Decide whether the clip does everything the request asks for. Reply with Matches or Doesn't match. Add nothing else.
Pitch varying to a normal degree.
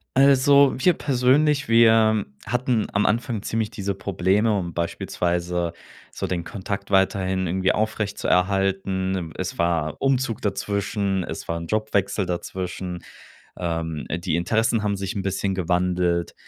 Matches